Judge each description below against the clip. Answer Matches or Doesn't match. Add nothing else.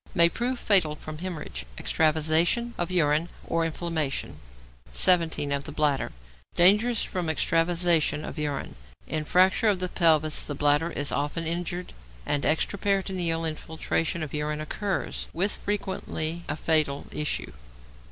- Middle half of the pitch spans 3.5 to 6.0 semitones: Doesn't match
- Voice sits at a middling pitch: Matches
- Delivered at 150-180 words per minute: Doesn't match